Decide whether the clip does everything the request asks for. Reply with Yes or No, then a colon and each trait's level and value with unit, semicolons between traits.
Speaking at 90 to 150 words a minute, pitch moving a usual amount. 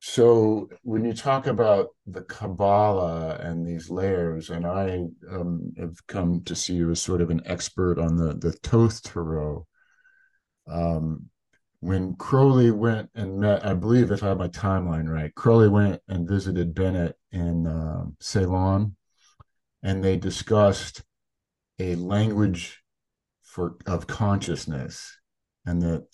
Yes: average, 140 wpm; average, 3.5 semitones